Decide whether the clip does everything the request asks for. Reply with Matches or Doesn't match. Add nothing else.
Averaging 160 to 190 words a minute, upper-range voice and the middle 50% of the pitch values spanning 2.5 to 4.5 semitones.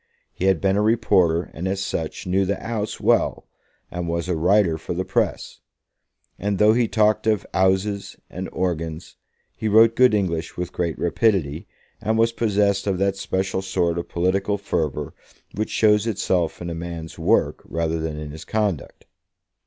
Doesn't match